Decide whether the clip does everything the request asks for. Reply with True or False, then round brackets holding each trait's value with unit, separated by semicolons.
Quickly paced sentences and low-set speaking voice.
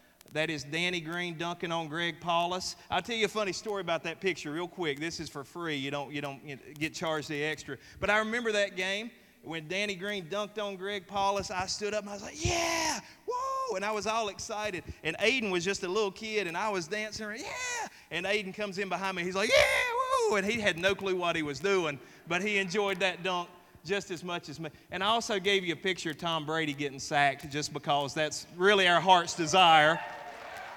False (230 wpm; 185 Hz)